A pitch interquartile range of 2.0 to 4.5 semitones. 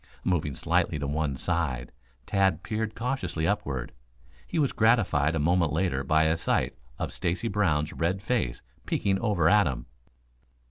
No: wide, 5.6 semitones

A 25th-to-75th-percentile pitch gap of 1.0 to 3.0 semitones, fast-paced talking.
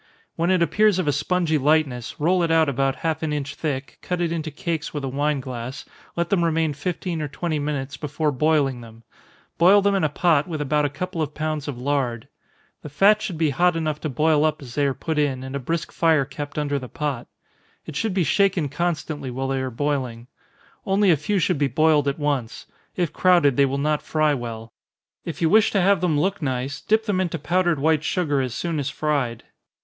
No: average, 3.4 semitones; fast, 220 wpm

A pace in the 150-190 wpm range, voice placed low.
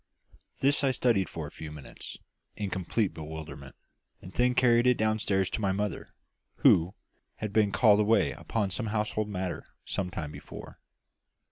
Yes: average, 155 wpm; low, 105 Hz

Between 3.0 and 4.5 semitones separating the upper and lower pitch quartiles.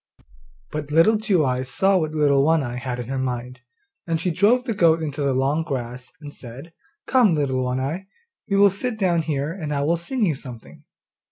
No: average, 5.3 semitones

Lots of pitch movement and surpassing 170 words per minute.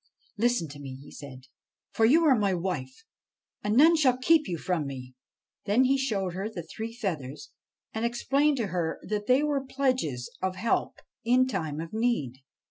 Yes: wide, 8.0 semitones; average, 190 wpm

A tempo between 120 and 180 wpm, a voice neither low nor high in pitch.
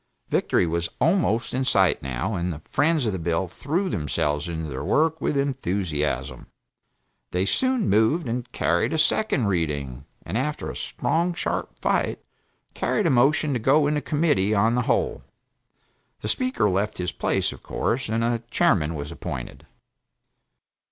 No: average, 160 wpm; low, 110 Hz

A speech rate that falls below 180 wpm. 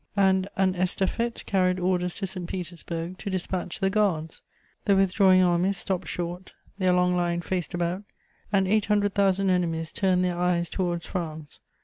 Yes: average, 160 wpm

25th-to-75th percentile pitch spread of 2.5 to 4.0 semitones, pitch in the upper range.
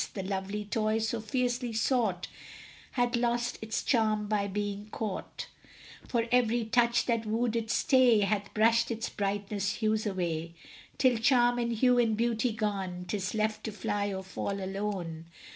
Yes: average, 2.8 semitones; high, 215 Hz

